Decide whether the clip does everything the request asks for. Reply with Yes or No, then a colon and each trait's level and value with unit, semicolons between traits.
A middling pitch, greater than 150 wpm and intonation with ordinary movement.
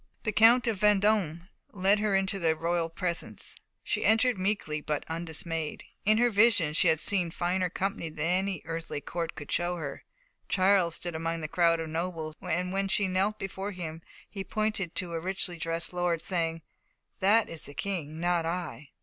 Yes: medium, 175 Hz; average, 180 wpm; average, 3.1 semitones